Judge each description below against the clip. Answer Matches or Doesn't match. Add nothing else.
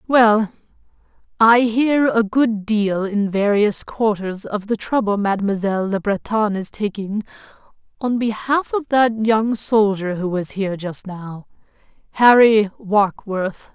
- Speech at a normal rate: Doesn't match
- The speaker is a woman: Matches